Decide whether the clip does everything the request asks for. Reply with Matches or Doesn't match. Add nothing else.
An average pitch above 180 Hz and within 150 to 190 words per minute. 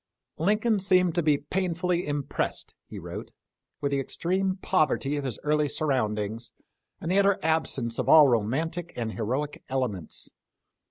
Doesn't match